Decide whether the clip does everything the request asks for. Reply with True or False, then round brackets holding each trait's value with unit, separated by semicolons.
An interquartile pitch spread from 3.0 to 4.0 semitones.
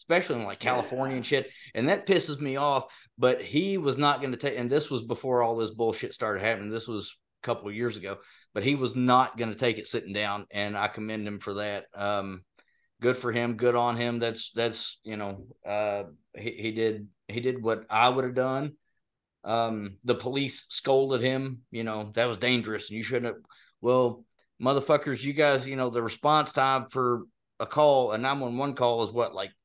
True (3.4 semitones)